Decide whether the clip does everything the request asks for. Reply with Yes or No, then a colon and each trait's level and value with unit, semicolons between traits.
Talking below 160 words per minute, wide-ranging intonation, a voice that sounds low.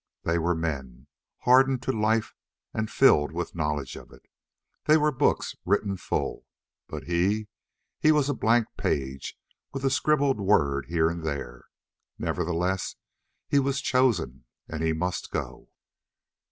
Yes: average, 140 wpm; wide, 8.3 semitones; very low, 95 Hz